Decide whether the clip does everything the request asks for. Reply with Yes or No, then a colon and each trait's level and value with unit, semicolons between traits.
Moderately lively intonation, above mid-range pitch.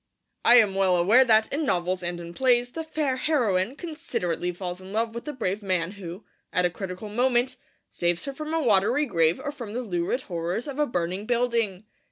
No: wide, 5.9 semitones; high, 215 Hz